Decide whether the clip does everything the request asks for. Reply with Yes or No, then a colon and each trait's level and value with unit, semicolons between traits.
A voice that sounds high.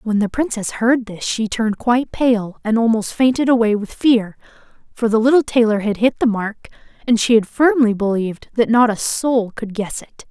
Yes: high, 225 Hz